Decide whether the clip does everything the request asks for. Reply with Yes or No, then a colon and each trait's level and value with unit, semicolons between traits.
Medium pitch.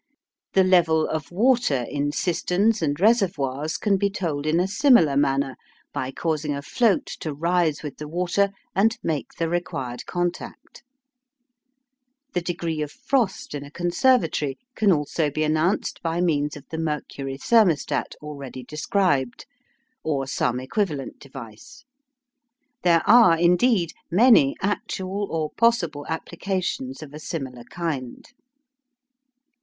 Yes: medium, 160 Hz